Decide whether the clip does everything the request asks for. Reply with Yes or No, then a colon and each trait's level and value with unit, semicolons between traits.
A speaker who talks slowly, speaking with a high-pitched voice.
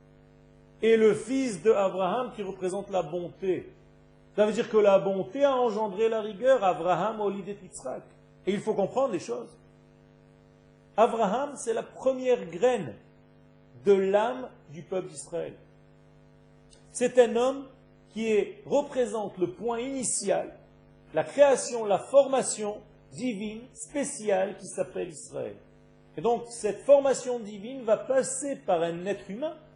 Yes: slow, 140 wpm; high, 220 Hz